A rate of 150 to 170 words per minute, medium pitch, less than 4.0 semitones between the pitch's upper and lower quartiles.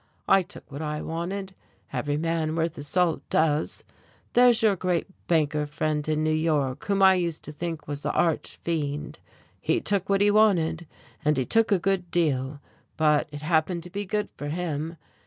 No: average, 185 wpm; medium, 165 Hz; average, 3.3 semitones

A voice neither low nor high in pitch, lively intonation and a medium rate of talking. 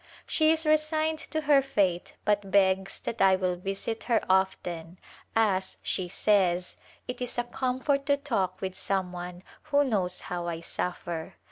No: high, 195 Hz; wide, 6.7 semitones; average, 170 wpm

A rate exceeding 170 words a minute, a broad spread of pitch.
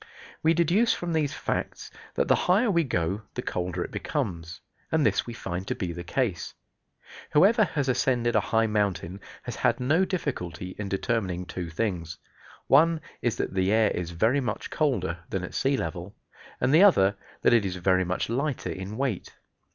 Yes: average, 180 wpm; wide, 8.0 semitones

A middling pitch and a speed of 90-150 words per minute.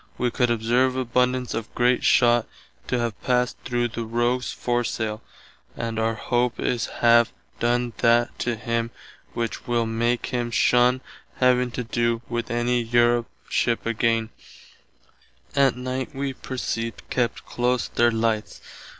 No: low, 120 Hz; average, 140 wpm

